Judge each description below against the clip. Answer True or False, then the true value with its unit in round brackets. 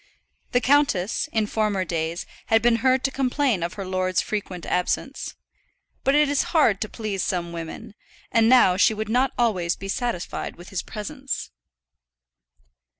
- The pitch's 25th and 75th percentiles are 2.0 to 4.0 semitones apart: False (5.6 semitones)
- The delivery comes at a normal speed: True (155 wpm)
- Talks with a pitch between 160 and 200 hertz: False (215 Hz)